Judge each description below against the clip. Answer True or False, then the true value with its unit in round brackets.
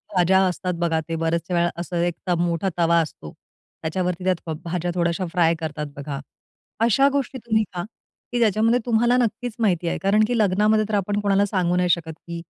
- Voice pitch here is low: False (180 Hz)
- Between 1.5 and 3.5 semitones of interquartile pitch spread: False (4.1 semitones)